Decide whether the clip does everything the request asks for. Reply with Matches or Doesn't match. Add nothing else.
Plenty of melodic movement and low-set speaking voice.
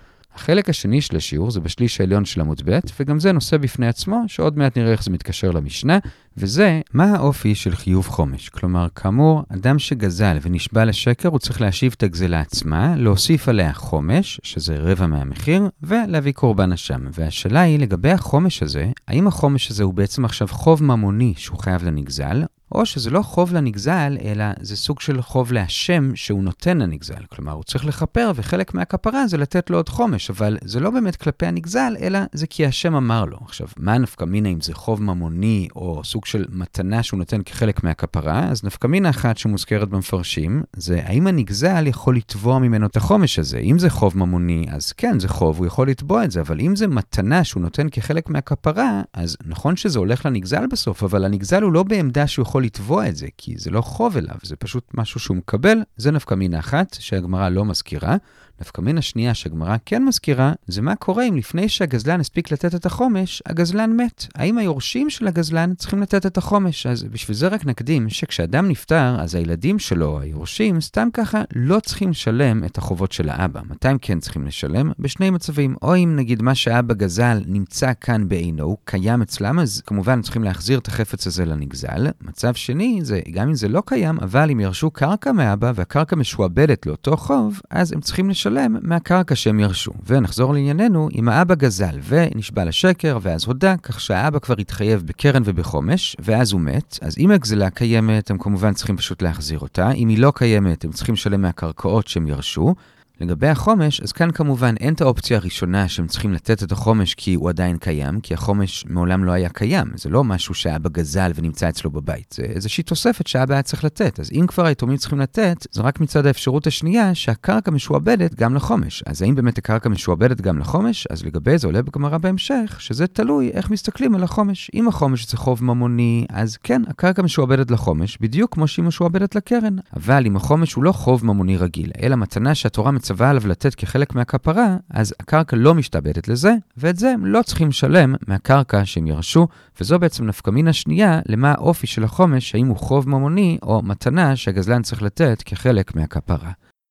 Matches